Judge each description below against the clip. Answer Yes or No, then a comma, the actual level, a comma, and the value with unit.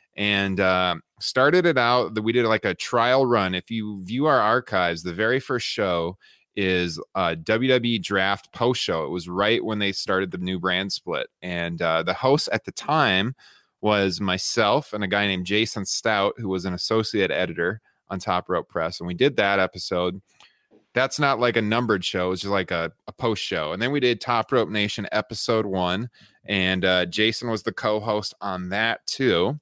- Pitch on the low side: Yes, low, 100 Hz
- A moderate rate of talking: Yes, average, 195 wpm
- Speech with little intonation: No, average, 3.8 semitones